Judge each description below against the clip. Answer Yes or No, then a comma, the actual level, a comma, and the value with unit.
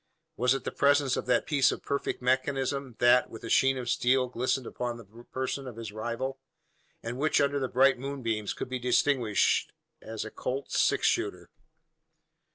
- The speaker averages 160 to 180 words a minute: Yes, average, 175 wpm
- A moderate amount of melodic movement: No, narrow, 2.2 semitones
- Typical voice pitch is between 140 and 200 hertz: No, low, 125 Hz